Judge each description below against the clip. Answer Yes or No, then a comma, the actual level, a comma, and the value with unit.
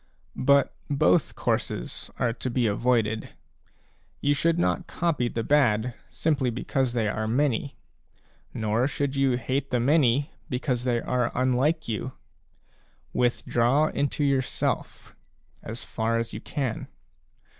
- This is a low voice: Yes, low, 125 Hz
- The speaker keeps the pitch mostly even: No, average, 3.3 semitones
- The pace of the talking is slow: Yes, slow, 125 wpm